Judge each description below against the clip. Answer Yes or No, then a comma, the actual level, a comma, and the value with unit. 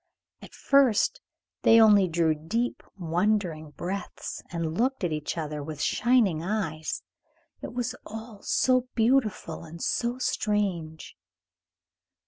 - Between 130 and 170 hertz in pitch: No, high, 195 Hz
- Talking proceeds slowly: Yes, slow, 115 wpm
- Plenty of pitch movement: Yes, wide, 6.1 semitones